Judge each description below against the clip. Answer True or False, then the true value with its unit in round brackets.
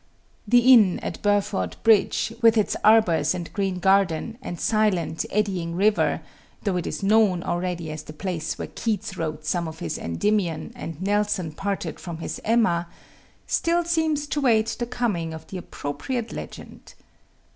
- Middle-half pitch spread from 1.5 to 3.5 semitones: False (4.7 semitones)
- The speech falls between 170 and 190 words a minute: False (155 wpm)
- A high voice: True (195 Hz)